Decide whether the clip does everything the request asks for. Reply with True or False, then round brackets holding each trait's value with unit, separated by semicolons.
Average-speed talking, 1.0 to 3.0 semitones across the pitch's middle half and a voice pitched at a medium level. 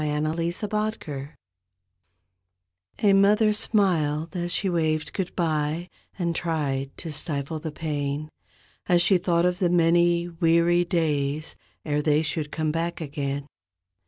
False (130 wpm; 2.6 semitones; 165 Hz)